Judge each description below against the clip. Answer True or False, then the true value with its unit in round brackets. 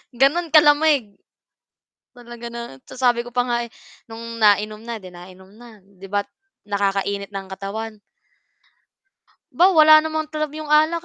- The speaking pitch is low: False (230 Hz)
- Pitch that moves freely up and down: True (6.5 semitones)